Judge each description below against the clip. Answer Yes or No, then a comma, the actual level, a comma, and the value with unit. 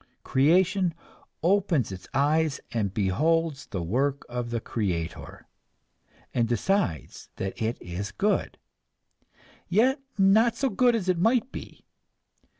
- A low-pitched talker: No, medium, 150 Hz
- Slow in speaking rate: Yes, slow, 120 wpm